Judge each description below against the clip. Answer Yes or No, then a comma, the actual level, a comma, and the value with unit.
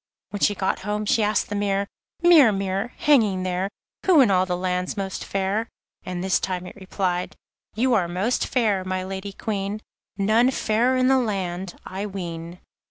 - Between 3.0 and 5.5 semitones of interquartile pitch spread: No, narrow, 2.6 semitones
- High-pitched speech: Yes, high, 195 Hz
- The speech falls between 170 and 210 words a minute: Yes, average, 175 wpm